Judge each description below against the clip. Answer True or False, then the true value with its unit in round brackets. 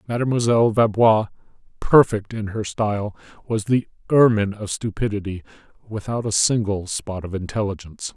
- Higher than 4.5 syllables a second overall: True (5.4 syllables/s)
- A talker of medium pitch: False (105 Hz)